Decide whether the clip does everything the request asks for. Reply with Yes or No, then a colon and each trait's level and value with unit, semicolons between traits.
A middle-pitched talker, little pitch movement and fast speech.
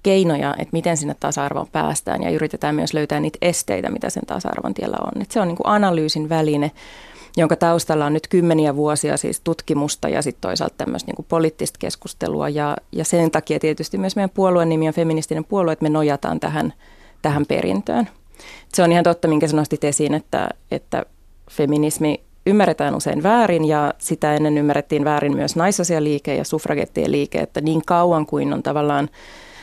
Yes: medium, 160 Hz; narrow, 2.3 semitones; fast, 175 wpm